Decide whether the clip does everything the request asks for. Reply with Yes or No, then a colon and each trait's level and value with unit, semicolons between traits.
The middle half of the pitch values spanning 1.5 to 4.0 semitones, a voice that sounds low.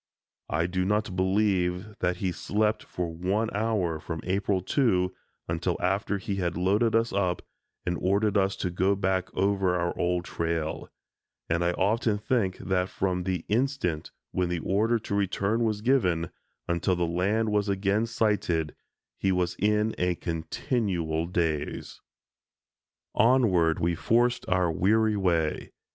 Yes: average, 3.3 semitones; very low, 95 Hz